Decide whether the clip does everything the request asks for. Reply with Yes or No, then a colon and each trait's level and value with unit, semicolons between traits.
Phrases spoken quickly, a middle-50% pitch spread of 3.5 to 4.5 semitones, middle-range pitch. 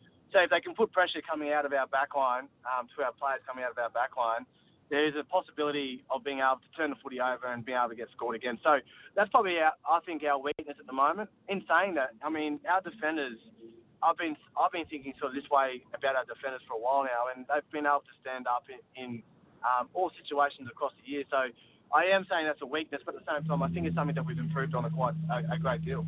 Yes: fast, 260 wpm; average, 3.9 semitones; medium, 145 Hz